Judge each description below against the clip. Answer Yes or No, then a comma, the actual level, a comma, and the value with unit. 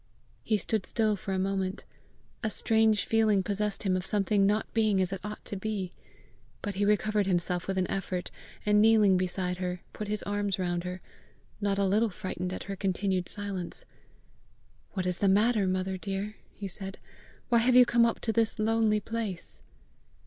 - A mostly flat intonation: Yes, narrow, 2.3 semitones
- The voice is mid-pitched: No, high, 200 Hz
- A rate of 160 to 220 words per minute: Yes, average, 180 wpm